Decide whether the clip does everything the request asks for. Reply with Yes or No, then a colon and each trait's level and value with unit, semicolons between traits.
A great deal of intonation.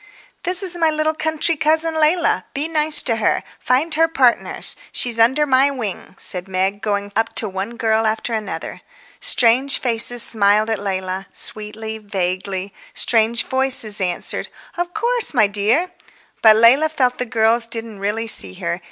Yes: wide, 6.4 semitones